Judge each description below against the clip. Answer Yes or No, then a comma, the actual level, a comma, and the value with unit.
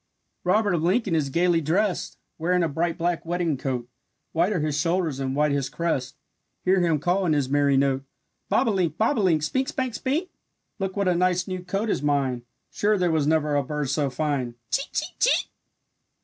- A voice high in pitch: No, medium, 165 Hz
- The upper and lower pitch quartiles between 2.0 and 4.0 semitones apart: No, average, 4.4 semitones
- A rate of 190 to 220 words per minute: Yes, average, 195 wpm